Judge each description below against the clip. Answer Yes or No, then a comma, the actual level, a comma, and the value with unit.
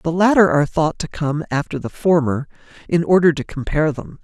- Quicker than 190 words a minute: Yes, average, 200 wpm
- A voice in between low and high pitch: Yes, medium, 160 Hz